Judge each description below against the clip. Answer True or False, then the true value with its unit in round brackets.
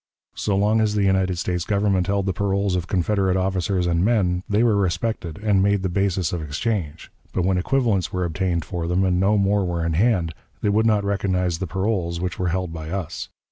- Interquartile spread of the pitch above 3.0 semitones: False (2.4 semitones)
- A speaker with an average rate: False (215 wpm)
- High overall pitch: False (95 Hz)